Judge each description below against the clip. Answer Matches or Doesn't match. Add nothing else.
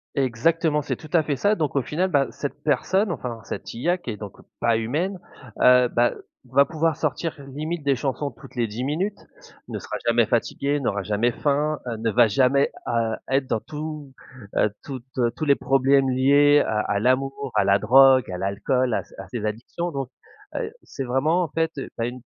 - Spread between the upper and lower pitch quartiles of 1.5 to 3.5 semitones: Doesn't match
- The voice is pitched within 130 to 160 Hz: Matches